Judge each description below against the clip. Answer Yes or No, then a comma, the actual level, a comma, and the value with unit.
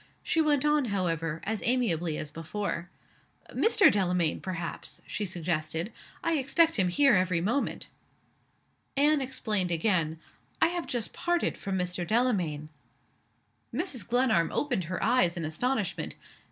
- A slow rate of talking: Yes, slow, 130 wpm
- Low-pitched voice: No, high, 195 Hz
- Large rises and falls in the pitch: Yes, wide, 7.4 semitones